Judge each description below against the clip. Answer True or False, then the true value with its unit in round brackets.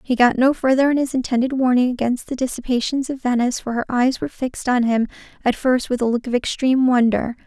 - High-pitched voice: True (250 Hz)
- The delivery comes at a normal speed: False (225 wpm)